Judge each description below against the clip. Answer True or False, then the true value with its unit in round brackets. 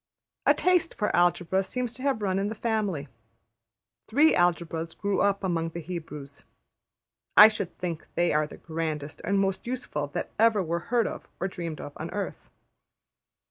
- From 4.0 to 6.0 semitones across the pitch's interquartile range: True (4.6 semitones)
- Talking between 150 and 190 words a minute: True (170 wpm)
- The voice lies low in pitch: False (180 Hz)